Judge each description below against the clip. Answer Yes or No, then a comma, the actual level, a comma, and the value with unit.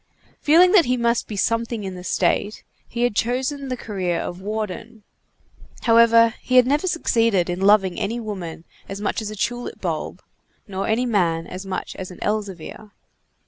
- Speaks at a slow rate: No, average, 175 wpm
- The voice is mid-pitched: No, high, 215 Hz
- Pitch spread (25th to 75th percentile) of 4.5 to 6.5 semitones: No, average, 3.9 semitones